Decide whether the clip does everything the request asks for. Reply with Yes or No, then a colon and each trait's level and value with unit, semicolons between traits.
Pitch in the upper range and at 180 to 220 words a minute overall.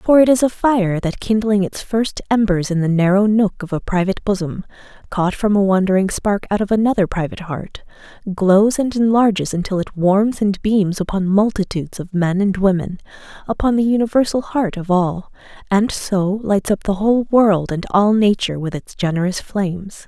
Yes: high, 200 Hz; average, 185 wpm